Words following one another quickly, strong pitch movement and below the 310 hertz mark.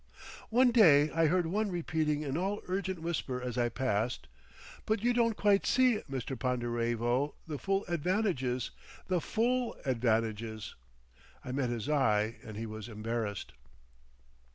No: average, 140 wpm; wide, 8.1 semitones; medium, 140 Hz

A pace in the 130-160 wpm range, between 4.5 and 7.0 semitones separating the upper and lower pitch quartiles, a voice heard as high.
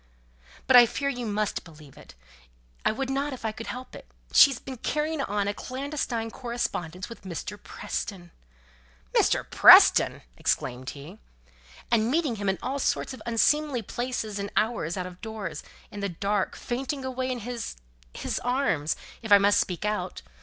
No: average, 170 wpm; average, 5.2 semitones; high, 220 Hz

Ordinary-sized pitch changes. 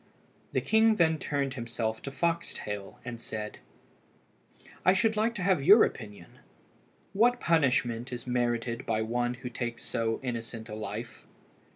No: wide, 6.5 semitones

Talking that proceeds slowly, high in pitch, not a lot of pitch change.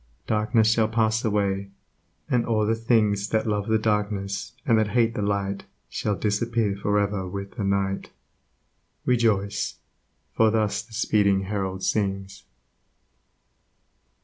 No: slow, 130 wpm; low, 105 Hz; narrow, 2.0 semitones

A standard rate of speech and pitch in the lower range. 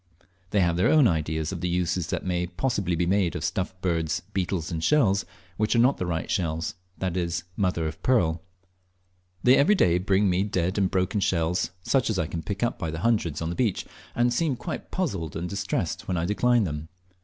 No: fast, 210 wpm; very low, 90 Hz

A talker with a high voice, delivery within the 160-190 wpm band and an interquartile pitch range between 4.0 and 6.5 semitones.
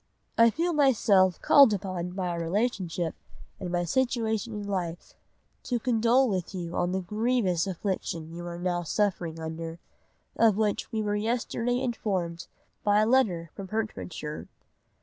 No: high, 195 Hz; average, 150 wpm; average, 4.7 semitones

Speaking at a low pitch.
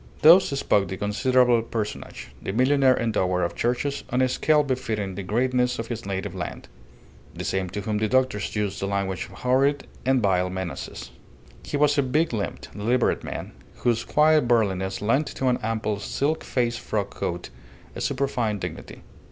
Yes: low, 115 Hz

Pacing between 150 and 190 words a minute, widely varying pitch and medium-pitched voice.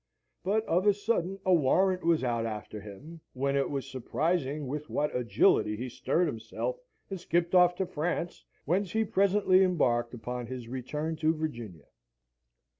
Yes: average, 160 wpm; wide, 6.4 semitones; medium, 155 Hz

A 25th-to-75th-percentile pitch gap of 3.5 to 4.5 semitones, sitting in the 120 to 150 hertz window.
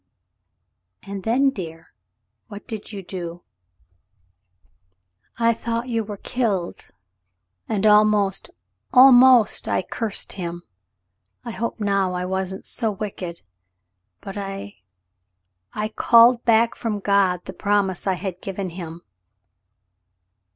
No: average, 4.0 semitones; high, 195 Hz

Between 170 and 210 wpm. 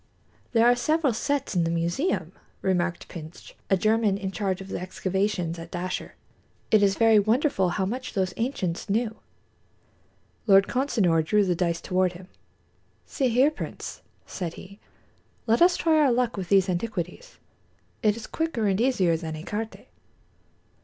No: average, 155 wpm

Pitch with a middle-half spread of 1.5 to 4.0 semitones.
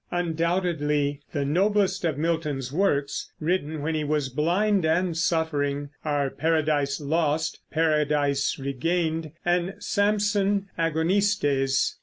Yes: average, 3.4 semitones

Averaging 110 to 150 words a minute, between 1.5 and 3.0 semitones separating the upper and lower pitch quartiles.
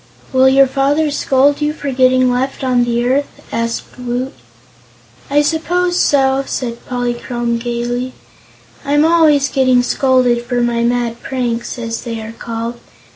Yes: average, 140 wpm; narrow, 2.4 semitones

